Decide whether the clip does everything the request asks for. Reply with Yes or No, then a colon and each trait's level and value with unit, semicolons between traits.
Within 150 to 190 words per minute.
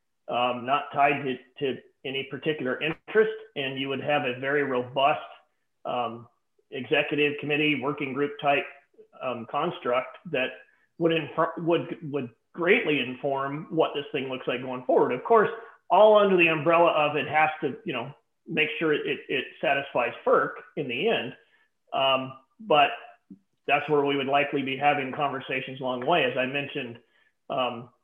Yes: average, 160 wpm